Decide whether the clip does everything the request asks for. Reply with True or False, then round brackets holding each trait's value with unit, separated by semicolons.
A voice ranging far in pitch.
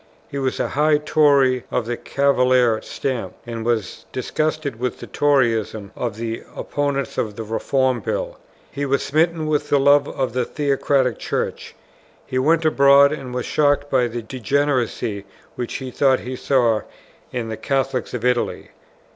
False (3.0 semitones)